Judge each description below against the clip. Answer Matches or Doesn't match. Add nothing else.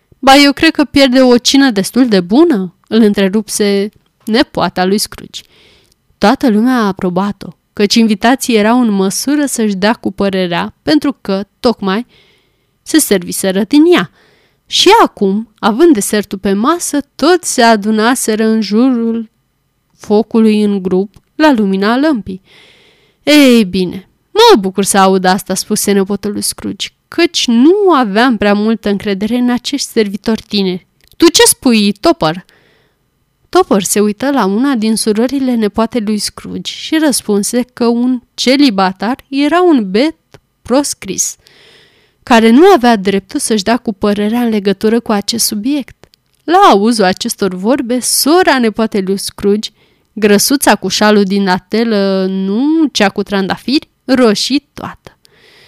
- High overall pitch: Matches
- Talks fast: Doesn't match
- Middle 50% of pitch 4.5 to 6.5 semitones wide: Matches